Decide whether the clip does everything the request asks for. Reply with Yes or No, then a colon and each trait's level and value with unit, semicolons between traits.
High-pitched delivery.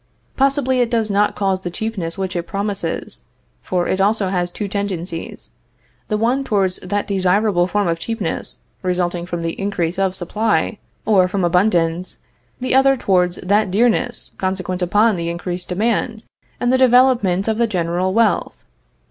Yes: high, 195 Hz